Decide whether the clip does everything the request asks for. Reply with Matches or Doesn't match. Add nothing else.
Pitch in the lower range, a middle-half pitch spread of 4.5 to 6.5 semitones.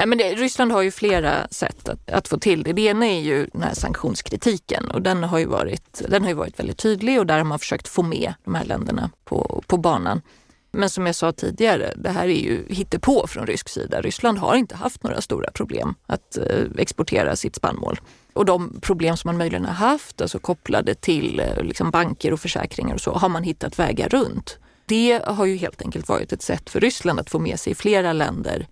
Doesn't match